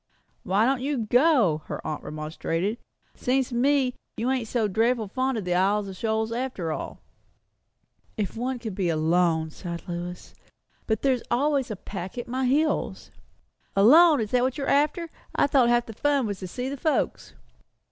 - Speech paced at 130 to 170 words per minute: No, average, 180 wpm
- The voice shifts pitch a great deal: Yes, wide, 5.7 semitones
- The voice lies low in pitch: No, high, 235 Hz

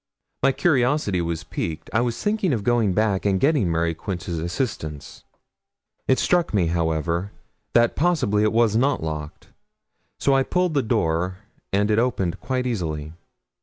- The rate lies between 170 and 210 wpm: No, average, 155 wpm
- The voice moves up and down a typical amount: No, wide, 7.2 semitones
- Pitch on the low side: Yes, low, 105 Hz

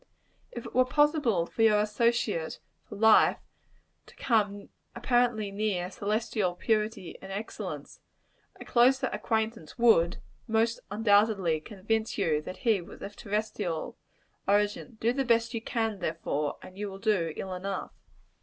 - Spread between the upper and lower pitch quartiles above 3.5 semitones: No, average, 3.1 semitones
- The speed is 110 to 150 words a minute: Yes, average, 140 wpm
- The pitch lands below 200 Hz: No, high, 210 Hz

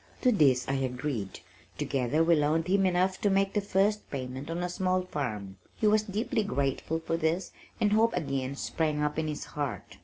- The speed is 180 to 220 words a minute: Yes, average, 190 wpm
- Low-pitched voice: No, medium, 160 Hz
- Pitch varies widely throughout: Yes, wide, 5.9 semitones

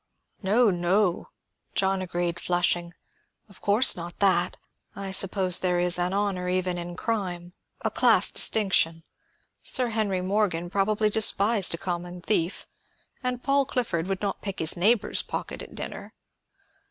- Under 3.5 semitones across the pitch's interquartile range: Yes, average, 2.9 semitones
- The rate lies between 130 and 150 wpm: Yes, average, 140 wpm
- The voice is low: No, high, 190 Hz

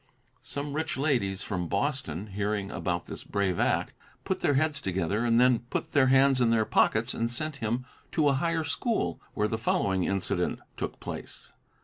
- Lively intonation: Yes, wide, 6.0 semitones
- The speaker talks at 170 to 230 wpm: Yes, average, 175 wpm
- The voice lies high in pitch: No, low, 115 Hz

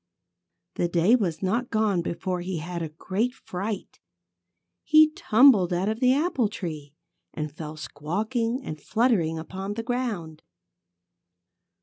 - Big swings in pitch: Yes, wide, 5.8 semitones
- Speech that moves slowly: Yes, slow, 130 wpm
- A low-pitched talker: No, high, 190 Hz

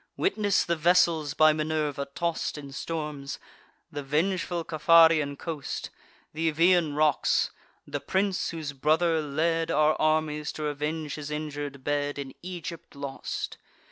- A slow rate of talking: Yes, slow, 130 wpm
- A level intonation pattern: Yes, narrow, 2.2 semitones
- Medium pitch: Yes, medium, 155 Hz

